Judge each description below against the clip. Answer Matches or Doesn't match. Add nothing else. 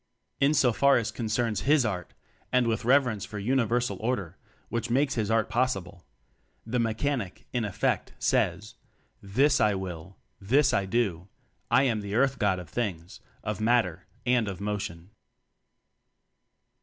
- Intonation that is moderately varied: Matches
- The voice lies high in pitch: Doesn't match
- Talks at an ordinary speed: Matches